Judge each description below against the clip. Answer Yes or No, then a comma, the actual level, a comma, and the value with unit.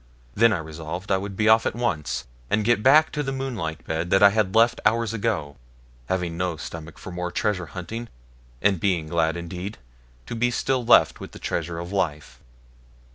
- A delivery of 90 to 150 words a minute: No, average, 190 wpm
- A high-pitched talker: No, very low, 95 Hz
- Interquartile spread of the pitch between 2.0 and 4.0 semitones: No, average, 5.2 semitones